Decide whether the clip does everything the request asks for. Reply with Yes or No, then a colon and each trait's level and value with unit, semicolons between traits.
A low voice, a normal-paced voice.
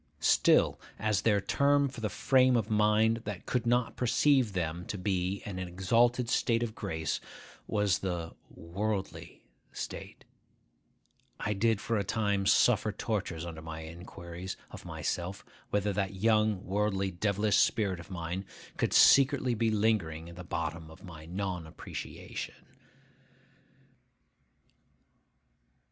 No: low, 100 Hz; slow, 130 wpm